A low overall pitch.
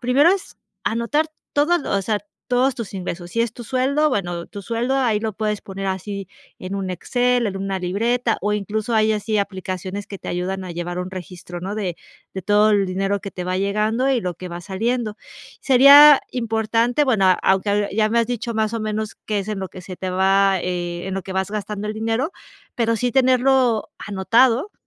No: high, 210 Hz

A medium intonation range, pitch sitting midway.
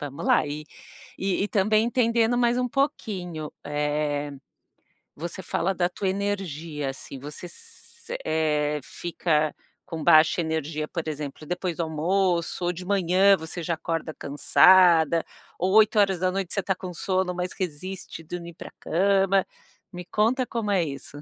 Yes: average, 3.9 semitones; medium, 175 Hz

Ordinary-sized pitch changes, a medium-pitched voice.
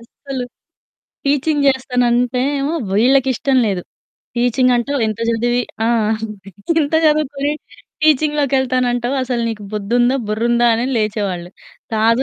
No: average, 3.2 semitones; high, 245 Hz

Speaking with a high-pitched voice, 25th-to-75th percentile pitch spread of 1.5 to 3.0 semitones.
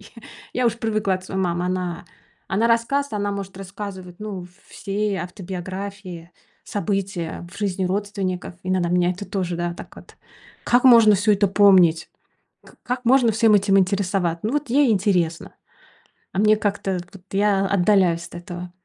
Yes: high, 195 Hz; average, 2.7 semitones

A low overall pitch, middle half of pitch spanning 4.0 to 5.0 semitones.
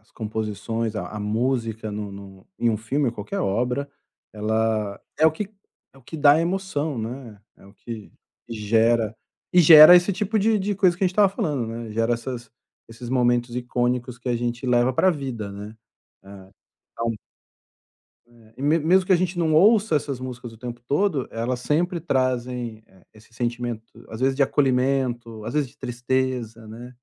Yes: low, 120 Hz; average, 4.5 semitones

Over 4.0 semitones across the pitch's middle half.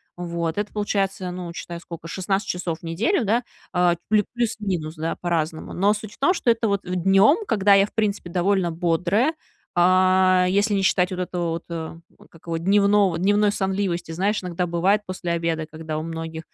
No: average, 3.2 semitones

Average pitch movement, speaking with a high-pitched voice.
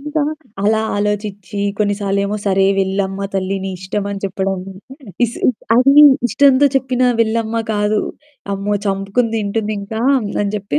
No: narrow, 2.2 semitones; high, 205 Hz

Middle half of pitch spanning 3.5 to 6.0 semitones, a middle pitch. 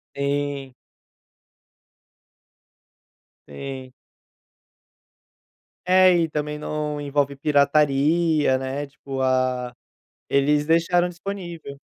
No: average, 2.8 semitones; medium, 145 Hz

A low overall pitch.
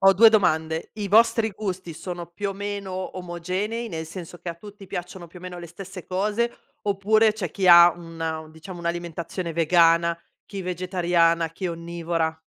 No: medium, 180 Hz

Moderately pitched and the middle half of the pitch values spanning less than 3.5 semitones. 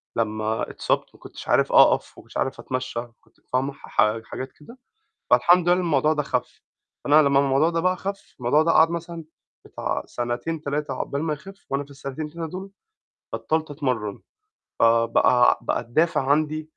No: medium, 145 Hz; average, 4.3 semitones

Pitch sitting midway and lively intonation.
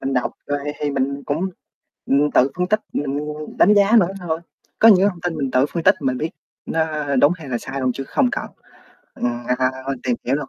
No: medium, 145 Hz; average, 4.2 semitones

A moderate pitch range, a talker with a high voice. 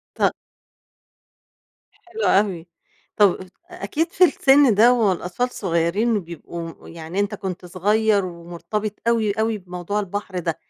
Yes: average, 3.9 semitones; high, 200 Hz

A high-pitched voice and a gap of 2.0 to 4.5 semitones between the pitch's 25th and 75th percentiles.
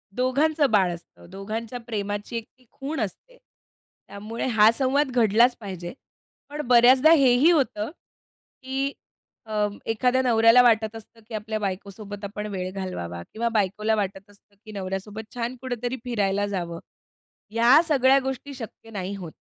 Yes: high, 225 Hz; average, 4.0 semitones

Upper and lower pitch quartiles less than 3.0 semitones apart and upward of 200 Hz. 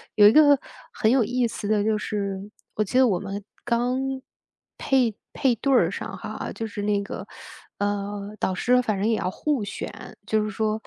No: average, 3.3 semitones; high, 215 Hz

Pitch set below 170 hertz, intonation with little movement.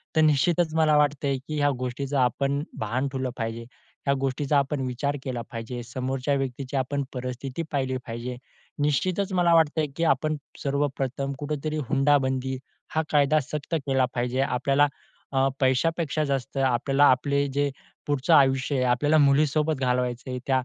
Yes: medium, 140 Hz; narrow, 2.2 semitones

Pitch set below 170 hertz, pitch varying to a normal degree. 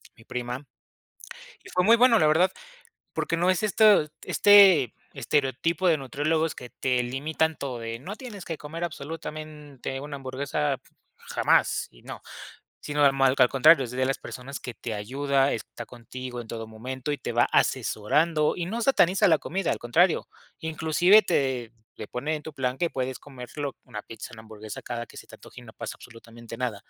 Yes: medium, 140 Hz; average, 4.7 semitones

